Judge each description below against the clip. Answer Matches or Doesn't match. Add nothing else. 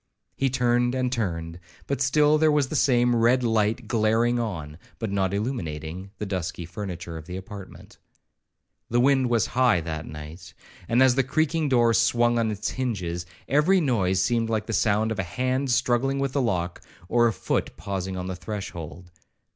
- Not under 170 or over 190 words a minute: Matches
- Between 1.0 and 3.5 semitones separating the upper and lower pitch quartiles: Doesn't match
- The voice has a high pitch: Doesn't match